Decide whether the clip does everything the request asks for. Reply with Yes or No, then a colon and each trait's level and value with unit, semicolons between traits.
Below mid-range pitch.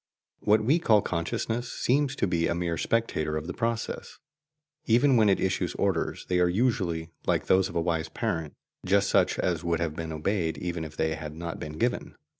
Yes: very low, 90 Hz